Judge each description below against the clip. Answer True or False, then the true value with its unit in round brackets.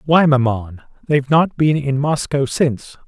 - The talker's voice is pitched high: False (140 Hz)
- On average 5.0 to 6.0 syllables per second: False (4.6 syllables/s)